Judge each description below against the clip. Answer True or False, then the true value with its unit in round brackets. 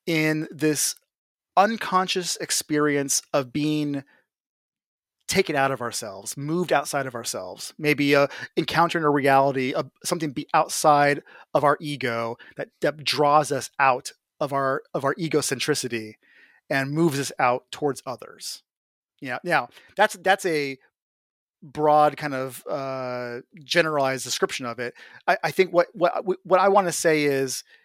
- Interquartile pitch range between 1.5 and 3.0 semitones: False (3.6 semitones)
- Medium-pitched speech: True (150 Hz)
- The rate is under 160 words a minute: True (145 wpm)